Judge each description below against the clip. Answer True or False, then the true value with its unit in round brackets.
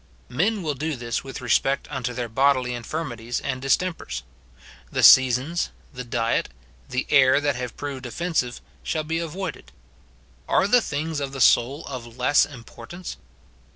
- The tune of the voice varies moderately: True (4.0 semitones)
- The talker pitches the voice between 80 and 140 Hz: True (135 Hz)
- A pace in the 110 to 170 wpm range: True (155 wpm)